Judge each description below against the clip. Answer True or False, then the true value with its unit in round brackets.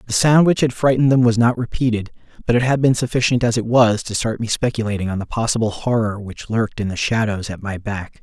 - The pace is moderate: False (240 wpm)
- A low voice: True (115 Hz)